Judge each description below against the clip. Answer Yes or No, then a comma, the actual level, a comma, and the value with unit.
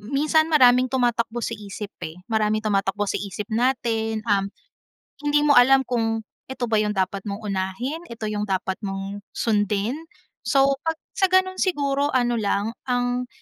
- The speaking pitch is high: Yes, high, 225 Hz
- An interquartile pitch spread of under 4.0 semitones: No, average, 4.4 semitones